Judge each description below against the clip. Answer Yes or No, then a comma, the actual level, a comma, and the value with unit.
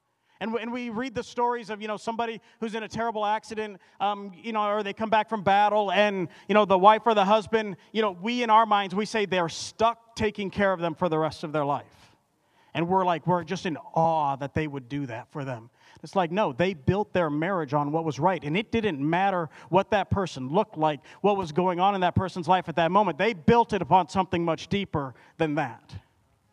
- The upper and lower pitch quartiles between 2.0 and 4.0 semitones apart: No, average, 4.8 semitones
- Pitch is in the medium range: No, high, 195 Hz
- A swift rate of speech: Yes, fast, 240 wpm